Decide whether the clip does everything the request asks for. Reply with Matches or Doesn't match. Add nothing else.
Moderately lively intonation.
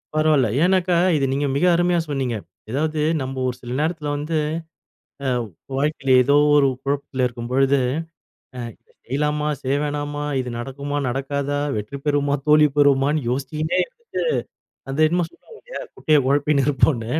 Doesn't match